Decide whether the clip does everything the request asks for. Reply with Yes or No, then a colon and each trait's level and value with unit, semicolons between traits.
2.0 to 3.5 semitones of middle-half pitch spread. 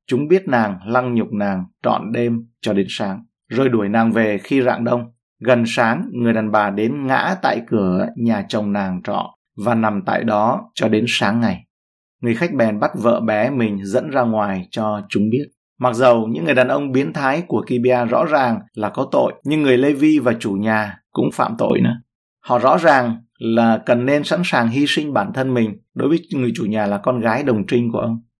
Yes: average, 3.0 semitones